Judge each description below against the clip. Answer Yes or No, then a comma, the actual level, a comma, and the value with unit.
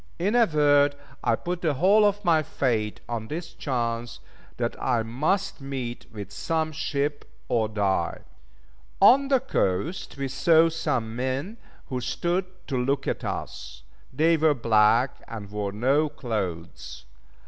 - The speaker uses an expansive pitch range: Yes, wide, 6.1 semitones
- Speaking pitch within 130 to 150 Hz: Yes, low, 135 Hz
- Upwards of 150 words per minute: No, average, 145 wpm